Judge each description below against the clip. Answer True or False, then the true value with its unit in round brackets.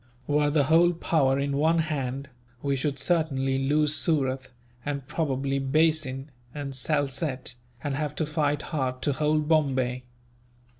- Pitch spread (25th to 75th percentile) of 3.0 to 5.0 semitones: False (2.4 semitones)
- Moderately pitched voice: True (145 Hz)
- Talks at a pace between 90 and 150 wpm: True (140 wpm)